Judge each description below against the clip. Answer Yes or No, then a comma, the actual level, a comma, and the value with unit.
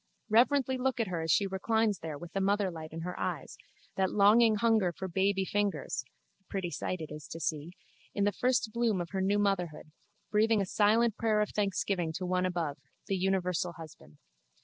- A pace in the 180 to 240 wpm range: Yes, average, 195 wpm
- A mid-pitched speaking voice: No, high, 195 Hz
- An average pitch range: Yes, average, 3.4 semitones